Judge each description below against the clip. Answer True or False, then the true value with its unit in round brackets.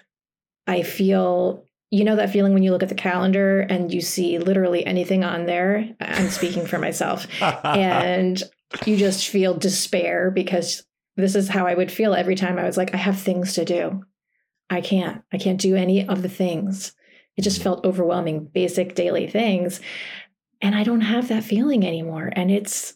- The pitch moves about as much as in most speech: False (1.7 semitones)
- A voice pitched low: False (185 Hz)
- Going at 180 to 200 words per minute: True (185 wpm)